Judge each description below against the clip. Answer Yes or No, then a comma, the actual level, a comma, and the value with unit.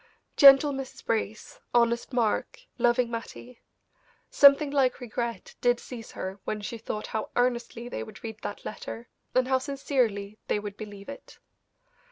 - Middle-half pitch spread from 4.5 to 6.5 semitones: No, average, 3.1 semitones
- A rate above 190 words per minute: No, average, 150 wpm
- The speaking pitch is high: Yes, high, 235 Hz